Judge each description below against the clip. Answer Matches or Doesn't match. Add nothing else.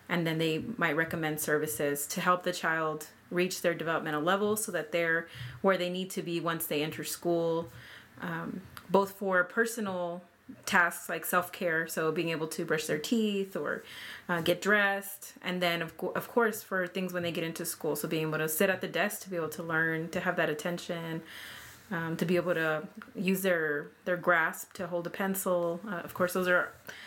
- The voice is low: Doesn't match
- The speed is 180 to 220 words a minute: Matches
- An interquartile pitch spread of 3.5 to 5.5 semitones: Doesn't match